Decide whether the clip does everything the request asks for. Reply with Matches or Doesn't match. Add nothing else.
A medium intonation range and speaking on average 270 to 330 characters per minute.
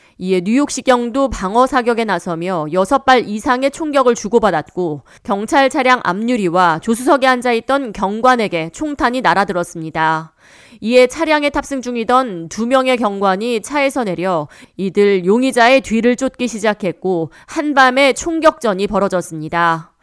Doesn't match